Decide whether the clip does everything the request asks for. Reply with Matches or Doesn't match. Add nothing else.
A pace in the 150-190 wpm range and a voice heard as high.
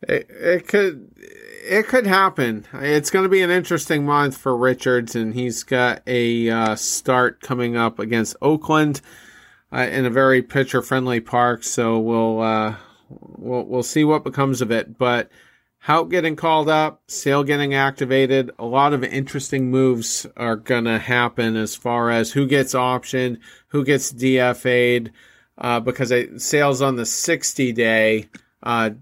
Doesn't match